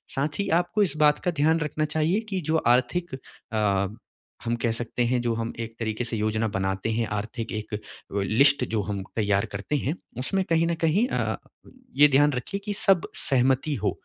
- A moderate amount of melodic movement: No, wide, 6.0 semitones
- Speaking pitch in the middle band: No, low, 125 Hz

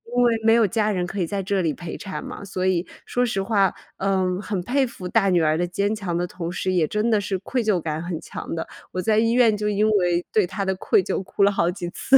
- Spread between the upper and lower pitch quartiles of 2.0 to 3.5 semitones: Yes, average, 3.2 semitones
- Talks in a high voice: Yes, high, 195 Hz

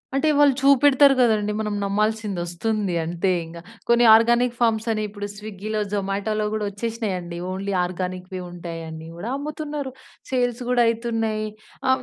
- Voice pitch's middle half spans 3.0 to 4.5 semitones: Yes, average, 3.9 semitones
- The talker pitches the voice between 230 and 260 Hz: No, high, 215 Hz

